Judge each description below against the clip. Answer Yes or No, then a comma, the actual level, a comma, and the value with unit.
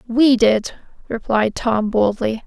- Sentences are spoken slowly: Yes, slow, 120 wpm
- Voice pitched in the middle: No, high, 230 Hz